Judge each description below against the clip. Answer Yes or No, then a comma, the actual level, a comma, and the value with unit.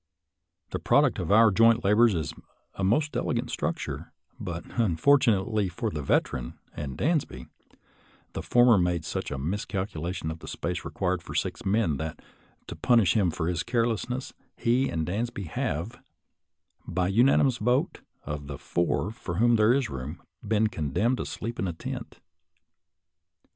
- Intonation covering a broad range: Yes, wide, 5.8 semitones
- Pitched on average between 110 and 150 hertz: No, low, 100 Hz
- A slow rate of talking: No, average, 155 wpm